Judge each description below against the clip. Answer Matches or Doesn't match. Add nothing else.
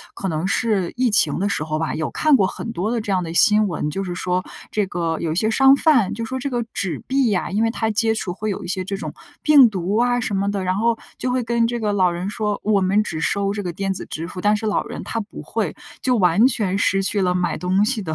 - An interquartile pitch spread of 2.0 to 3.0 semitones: Doesn't match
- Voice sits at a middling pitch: Doesn't match